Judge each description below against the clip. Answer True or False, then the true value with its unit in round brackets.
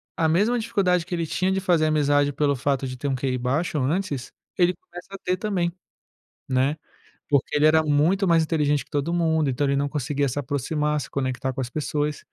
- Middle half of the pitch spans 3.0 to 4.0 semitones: True (3.6 semitones)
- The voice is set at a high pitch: False (150 Hz)